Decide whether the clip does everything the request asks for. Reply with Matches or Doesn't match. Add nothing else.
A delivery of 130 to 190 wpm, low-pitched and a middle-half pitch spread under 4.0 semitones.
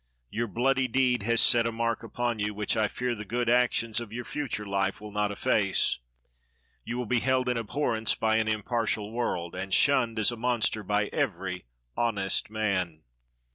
Matches